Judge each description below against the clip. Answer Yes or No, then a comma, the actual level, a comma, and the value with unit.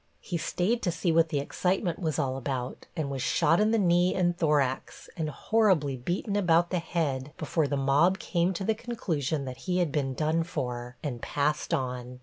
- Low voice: No, medium, 160 Hz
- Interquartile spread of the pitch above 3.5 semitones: Yes, average, 4.5 semitones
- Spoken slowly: No, average, 195 wpm